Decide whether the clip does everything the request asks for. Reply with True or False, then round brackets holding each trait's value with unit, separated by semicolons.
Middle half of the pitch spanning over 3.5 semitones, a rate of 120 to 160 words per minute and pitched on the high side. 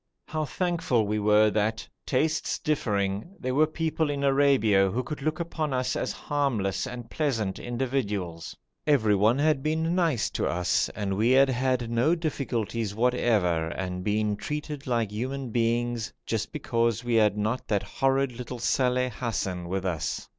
False (4.7 semitones; 155 wpm; 120 Hz)